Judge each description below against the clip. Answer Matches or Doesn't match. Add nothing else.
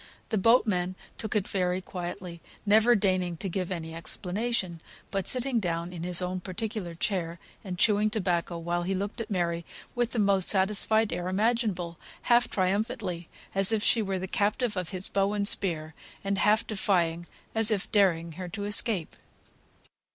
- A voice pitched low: Doesn't match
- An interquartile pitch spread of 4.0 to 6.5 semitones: Doesn't match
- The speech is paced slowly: Doesn't match